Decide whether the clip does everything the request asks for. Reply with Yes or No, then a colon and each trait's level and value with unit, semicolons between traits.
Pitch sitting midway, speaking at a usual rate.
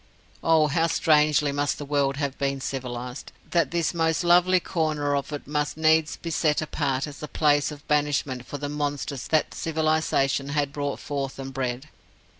Yes: medium, 145 Hz; average, 175 wpm